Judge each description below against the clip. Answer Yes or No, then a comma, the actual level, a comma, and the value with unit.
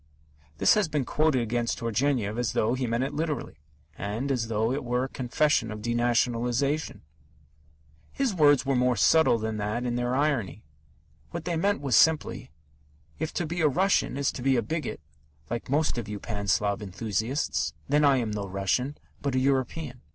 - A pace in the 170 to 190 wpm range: Yes, average, 180 wpm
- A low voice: Yes, low, 125 Hz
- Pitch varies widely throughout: No, average, 4.4 semitones